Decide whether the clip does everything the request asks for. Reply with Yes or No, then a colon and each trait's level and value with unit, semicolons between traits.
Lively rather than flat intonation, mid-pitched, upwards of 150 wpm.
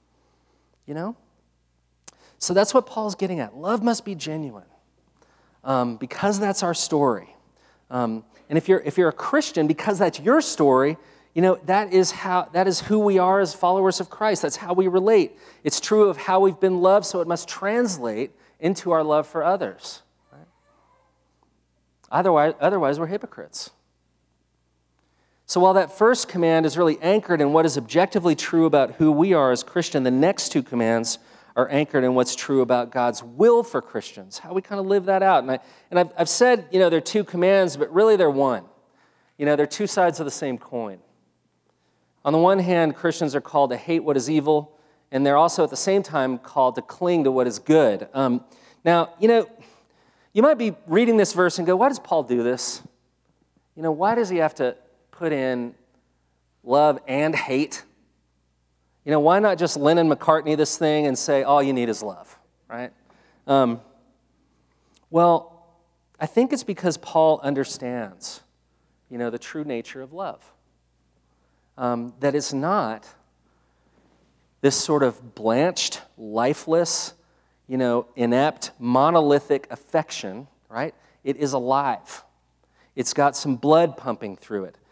Yes: wide, 6.9 semitones; medium, 150 Hz; average, 175 wpm